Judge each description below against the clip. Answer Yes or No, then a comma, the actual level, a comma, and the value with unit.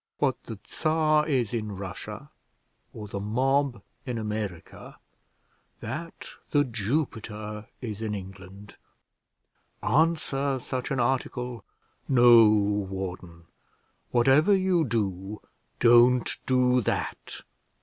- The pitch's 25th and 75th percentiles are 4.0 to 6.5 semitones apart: Yes, average, 4.5 semitones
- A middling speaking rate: No, slow, 100 wpm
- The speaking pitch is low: Yes, low, 120 Hz